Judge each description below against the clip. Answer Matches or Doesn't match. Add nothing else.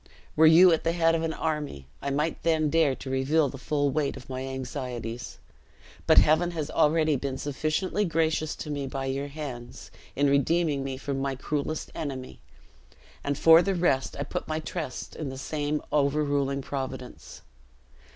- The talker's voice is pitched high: Doesn't match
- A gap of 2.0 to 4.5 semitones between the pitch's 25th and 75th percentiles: Matches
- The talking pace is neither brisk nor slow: Matches